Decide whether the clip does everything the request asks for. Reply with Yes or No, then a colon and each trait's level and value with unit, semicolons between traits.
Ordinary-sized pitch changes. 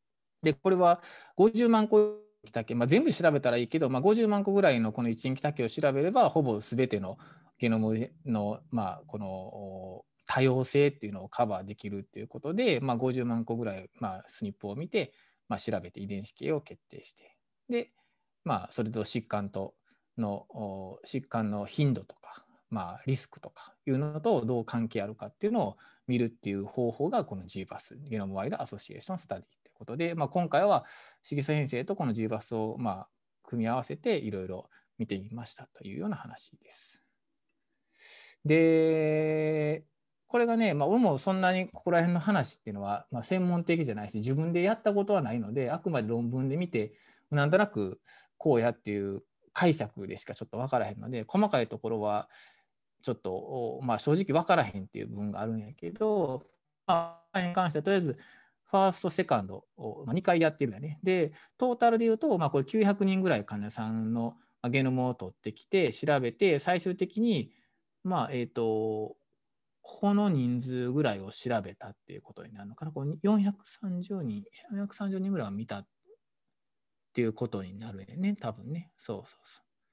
No: wide, 8.5 semitones